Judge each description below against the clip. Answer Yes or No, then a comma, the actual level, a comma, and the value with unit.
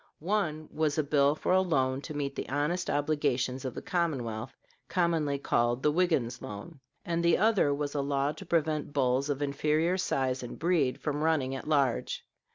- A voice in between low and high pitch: Yes, medium, 145 Hz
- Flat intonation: No, average, 3.3 semitones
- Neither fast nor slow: Yes, average, 180 wpm